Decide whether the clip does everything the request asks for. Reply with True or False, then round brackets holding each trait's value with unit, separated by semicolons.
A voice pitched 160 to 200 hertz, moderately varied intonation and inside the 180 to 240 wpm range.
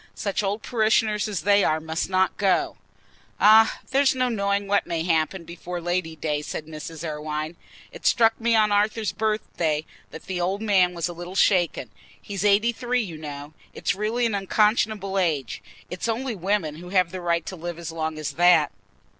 True (185 Hz; 4.5 semitones; 185 wpm)